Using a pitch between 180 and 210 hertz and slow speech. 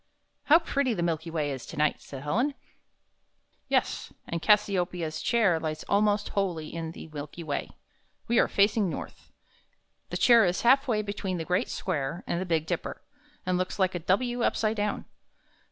No: medium, 185 Hz; average, 185 wpm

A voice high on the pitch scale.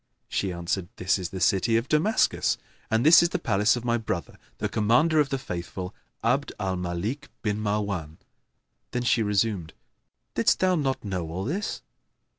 No: low, 105 Hz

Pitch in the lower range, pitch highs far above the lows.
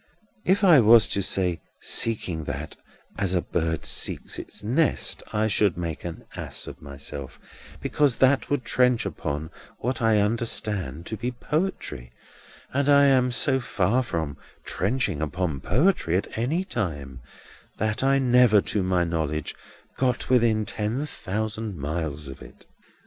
Yes: low, 105 Hz; wide, 7.2 semitones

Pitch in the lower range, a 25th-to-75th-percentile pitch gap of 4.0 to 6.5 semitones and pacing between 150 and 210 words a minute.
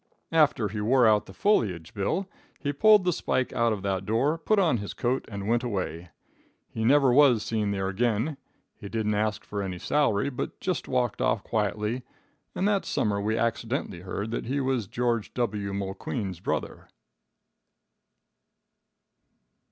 Yes: low, 115 Hz; average, 4.7 semitones; average, 160 wpm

